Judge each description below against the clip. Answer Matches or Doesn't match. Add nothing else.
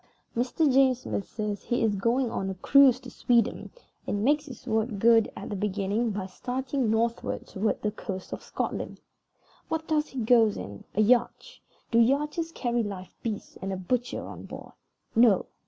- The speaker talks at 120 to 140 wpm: Doesn't match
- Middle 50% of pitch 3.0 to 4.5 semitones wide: Matches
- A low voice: Doesn't match